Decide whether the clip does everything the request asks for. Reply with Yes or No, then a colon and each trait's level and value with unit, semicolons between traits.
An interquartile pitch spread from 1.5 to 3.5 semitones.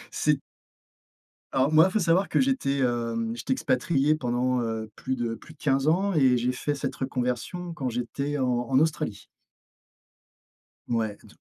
No: average, 4.2 semitones